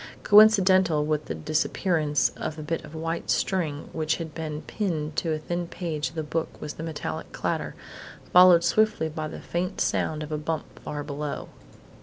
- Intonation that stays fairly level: Yes, narrow, 2.2 semitones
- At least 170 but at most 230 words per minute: Yes, average, 180 wpm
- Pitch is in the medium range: Yes, medium, 160 Hz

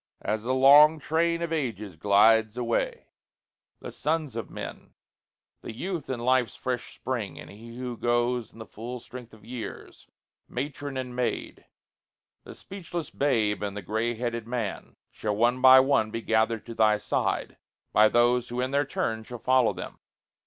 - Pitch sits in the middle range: No, low, 120 Hz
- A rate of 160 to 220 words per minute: Yes, average, 165 wpm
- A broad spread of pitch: No, average, 2.8 semitones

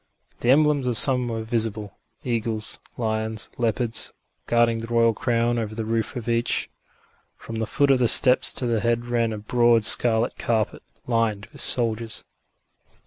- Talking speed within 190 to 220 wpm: No, average, 160 wpm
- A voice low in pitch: Yes, low, 115 Hz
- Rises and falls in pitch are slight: Yes, narrow, 1.3 semitones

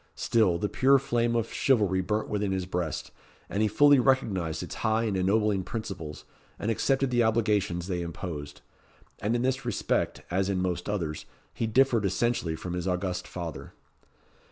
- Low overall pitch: Yes, low, 100 Hz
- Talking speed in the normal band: Yes, average, 165 wpm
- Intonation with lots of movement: No, average, 4.5 semitones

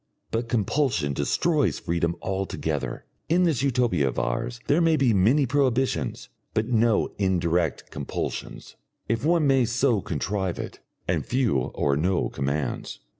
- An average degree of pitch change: No, wide, 7.3 semitones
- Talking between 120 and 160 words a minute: Yes, slow, 135 wpm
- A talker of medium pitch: No, low, 115 Hz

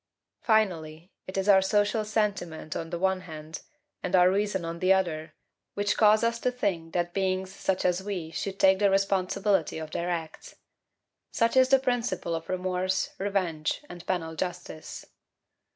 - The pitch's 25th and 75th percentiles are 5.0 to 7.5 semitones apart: No, average, 3.2 semitones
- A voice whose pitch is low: No, medium, 185 Hz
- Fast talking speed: No, average, 165 wpm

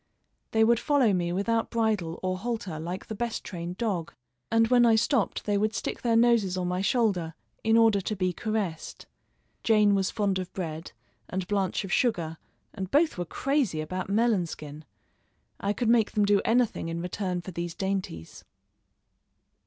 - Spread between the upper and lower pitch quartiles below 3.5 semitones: No, average, 4.1 semitones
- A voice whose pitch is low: No, high, 200 Hz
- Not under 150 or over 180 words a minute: Yes, average, 175 wpm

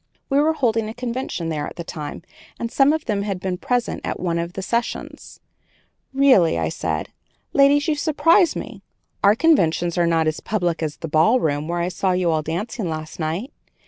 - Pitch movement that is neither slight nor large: No, wide, 7.4 semitones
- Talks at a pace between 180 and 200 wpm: Yes, average, 195 wpm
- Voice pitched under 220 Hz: Yes, medium, 185 Hz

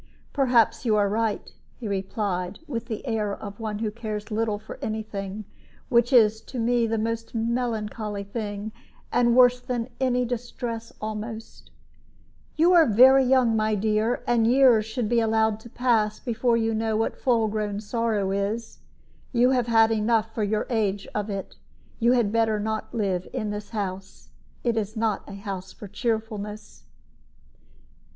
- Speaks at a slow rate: No, average, 160 wpm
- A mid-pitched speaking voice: No, high, 220 Hz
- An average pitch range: No, narrow, 2.0 semitones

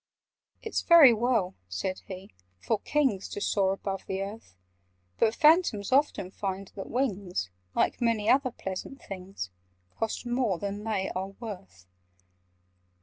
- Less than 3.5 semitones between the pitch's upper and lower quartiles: No, average, 4.2 semitones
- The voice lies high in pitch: Yes, high, 200 Hz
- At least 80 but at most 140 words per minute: Yes, slow, 135 wpm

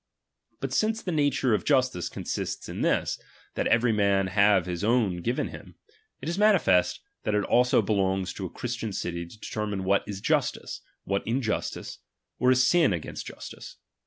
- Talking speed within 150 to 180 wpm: Yes, average, 175 wpm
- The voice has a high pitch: No, low, 105 Hz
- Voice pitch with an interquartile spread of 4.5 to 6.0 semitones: Yes, average, 4.8 semitones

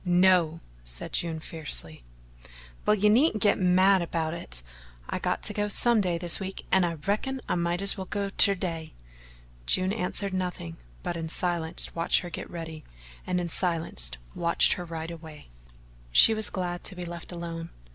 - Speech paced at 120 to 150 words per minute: No, average, 175 wpm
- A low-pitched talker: No, medium, 175 Hz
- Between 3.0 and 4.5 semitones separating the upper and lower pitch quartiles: No, narrow, 2.5 semitones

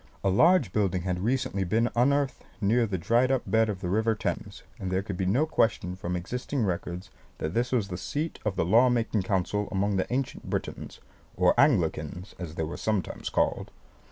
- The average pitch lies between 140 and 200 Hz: No, low, 105 Hz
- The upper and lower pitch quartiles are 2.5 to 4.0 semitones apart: No, average, 4.8 semitones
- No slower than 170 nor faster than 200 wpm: Yes, average, 195 wpm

